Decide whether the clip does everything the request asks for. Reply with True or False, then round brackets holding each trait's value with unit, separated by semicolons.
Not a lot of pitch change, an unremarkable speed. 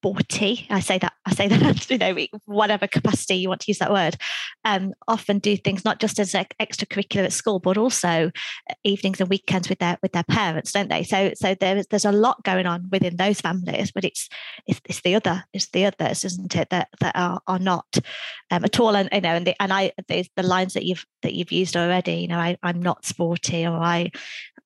False (2.3 semitones; 230 wpm)